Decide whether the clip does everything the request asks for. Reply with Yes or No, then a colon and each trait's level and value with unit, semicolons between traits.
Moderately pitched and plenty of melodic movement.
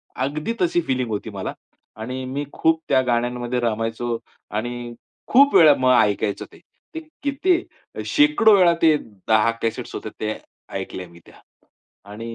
No: low, 125 Hz; wide, 6.3 semitones